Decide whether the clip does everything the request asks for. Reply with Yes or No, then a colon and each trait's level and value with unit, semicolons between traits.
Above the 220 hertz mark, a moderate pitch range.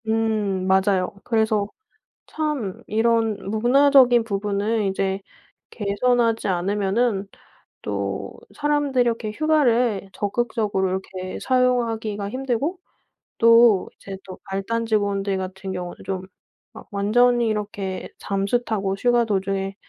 No: high, 215 Hz; average, 3.5 semitones